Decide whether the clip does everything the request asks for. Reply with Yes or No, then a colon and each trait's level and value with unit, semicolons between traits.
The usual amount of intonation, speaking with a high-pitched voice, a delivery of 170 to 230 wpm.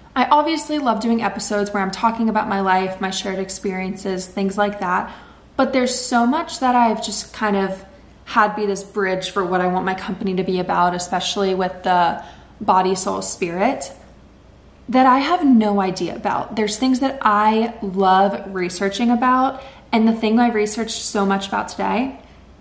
Yes: average, 3.7 semitones; high, 205 Hz; average, 180 wpm